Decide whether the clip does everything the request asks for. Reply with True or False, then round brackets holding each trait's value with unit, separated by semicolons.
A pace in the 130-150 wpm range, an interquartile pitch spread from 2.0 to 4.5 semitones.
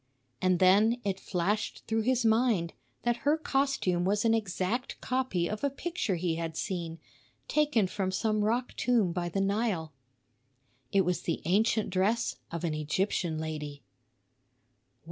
False (145 wpm; 5.0 semitones)